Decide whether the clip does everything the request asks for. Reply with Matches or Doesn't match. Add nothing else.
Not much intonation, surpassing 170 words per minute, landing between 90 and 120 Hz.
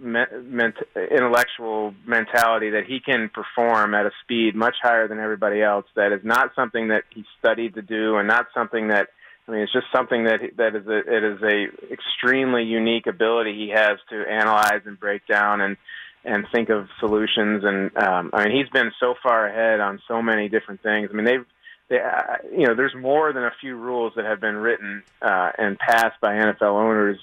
Matches